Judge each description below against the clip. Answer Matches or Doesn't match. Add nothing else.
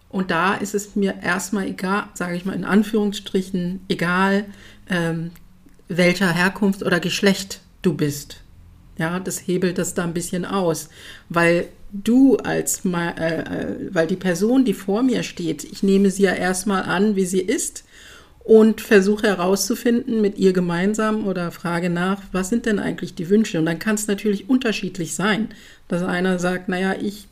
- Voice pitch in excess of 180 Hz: Matches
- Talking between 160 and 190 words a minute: Matches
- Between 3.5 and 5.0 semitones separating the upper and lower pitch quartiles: Doesn't match